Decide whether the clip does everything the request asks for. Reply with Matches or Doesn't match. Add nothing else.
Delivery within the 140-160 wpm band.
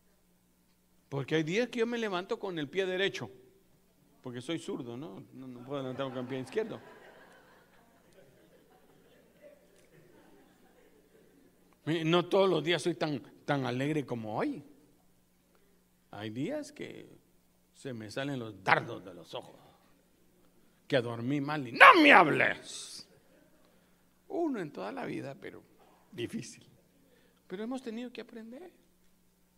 Doesn't match